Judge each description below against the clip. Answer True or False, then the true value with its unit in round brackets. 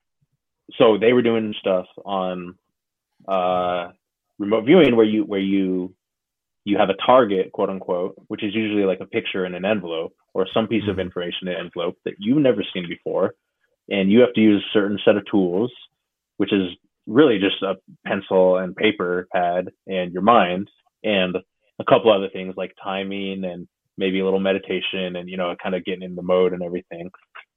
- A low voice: True (95 Hz)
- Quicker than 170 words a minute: True (185 wpm)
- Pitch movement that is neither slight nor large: False (2.2 semitones)